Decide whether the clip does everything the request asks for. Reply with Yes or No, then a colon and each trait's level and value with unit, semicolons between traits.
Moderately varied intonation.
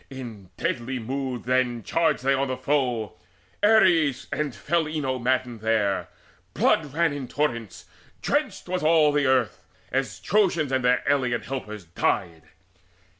Yes: average, 4.0 semitones